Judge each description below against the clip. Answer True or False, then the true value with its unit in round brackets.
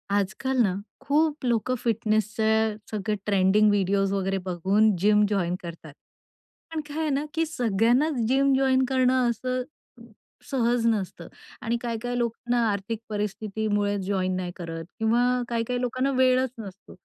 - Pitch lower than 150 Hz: False (220 Hz)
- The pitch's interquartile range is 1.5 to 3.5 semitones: False (4.0 semitones)